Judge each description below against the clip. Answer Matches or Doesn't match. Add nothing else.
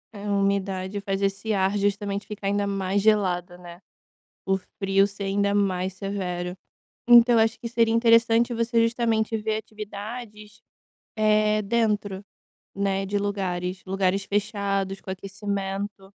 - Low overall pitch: Doesn't match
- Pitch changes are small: Matches